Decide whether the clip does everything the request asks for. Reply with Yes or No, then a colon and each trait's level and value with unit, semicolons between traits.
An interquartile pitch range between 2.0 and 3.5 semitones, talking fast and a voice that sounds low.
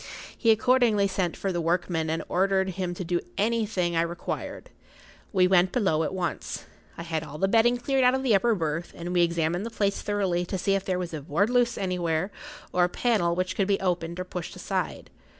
No: average, 3.1 semitones; fast, 220 wpm; medium, 185 Hz